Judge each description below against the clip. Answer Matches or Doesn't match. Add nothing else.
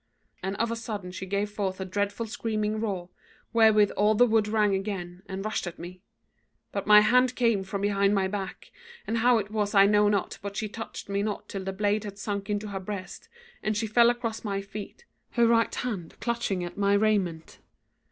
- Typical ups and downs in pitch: Doesn't match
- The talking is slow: Doesn't match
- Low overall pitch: Doesn't match